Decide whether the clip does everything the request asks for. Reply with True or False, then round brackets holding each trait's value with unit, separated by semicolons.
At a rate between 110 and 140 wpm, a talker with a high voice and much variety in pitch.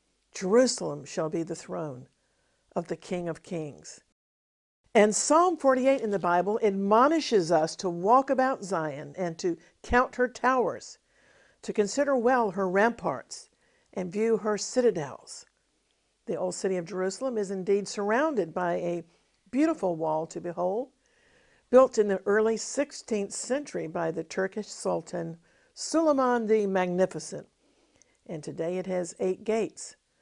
True (135 wpm; 200 Hz; 6.3 semitones)